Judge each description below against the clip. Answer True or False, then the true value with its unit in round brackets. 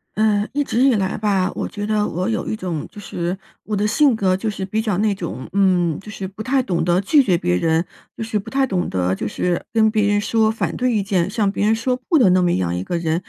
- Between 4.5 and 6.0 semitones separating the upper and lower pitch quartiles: False (3.6 semitones)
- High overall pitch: True (200 Hz)